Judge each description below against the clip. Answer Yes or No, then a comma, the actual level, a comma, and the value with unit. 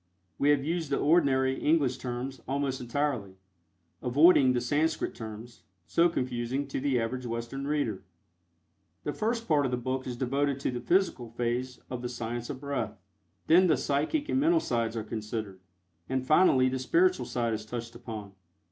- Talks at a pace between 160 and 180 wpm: Yes, average, 170 wpm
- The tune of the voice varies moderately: Yes, average, 3.4 semitones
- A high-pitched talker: No, low, 130 Hz